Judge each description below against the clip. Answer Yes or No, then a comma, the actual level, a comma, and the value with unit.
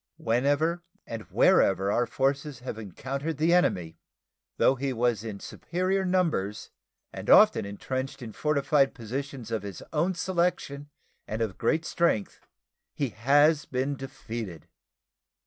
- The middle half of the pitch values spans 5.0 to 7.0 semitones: Yes, average, 5.3 semitones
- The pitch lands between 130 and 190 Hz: Yes, low, 135 Hz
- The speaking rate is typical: No, slow, 130 wpm